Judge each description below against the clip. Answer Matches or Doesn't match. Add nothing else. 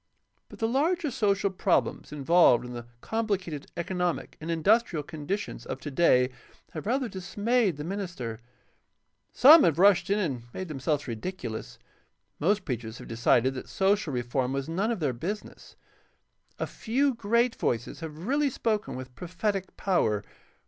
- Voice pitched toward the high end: Doesn't match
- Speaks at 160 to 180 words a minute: Doesn't match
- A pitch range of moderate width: Doesn't match